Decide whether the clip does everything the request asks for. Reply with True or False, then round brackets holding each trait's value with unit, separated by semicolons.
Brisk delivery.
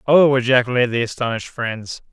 False (140 wpm)